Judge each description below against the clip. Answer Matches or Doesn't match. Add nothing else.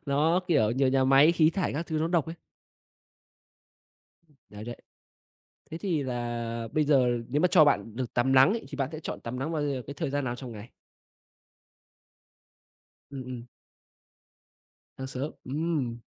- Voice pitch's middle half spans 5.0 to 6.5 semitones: Doesn't match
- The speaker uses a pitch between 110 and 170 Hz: Matches